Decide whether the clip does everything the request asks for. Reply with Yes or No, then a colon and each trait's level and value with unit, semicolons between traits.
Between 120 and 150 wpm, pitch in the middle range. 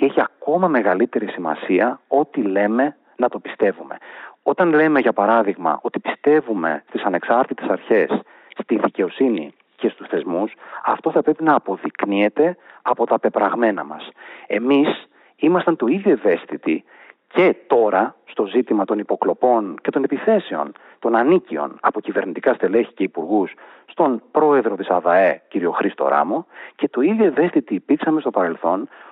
Yes: average, 140 wpm; medium, 150 Hz